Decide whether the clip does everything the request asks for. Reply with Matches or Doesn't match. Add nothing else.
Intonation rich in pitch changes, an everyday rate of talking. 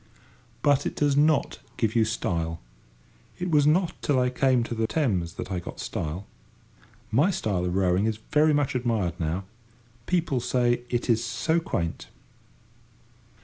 Matches